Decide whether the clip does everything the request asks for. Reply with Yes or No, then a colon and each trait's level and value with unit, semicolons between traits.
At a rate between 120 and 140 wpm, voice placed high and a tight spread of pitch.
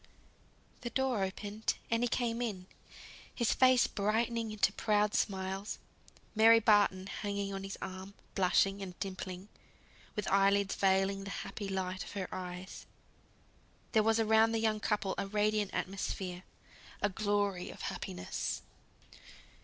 Yes: slow, 135 wpm; high, 200 Hz; narrow, 2.3 semitones